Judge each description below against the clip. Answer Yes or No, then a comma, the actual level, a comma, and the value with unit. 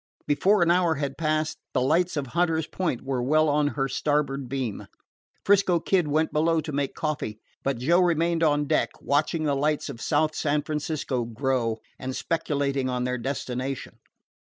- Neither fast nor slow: Yes, average, 170 wpm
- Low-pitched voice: No, medium, 145 Hz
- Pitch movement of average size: Yes, average, 3.1 semitones